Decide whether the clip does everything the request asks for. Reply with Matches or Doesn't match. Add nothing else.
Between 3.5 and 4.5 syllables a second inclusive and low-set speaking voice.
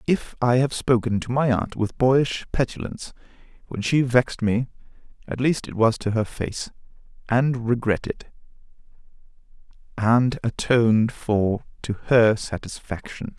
Matches